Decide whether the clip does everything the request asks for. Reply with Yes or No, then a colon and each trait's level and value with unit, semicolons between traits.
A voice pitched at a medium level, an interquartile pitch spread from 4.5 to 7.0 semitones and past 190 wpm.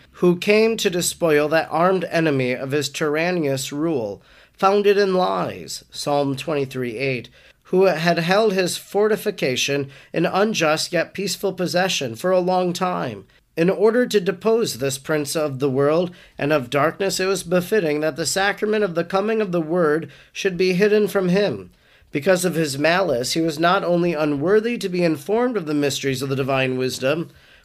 No: medium, 170 Hz; average, 4.9 semitones; average, 170 wpm